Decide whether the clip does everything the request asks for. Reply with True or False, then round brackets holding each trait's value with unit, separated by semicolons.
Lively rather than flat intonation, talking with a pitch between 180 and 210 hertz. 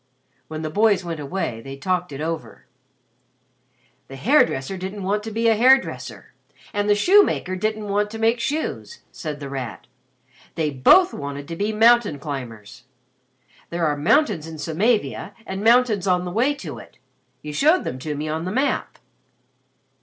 True (7.0 semitones; 185 Hz)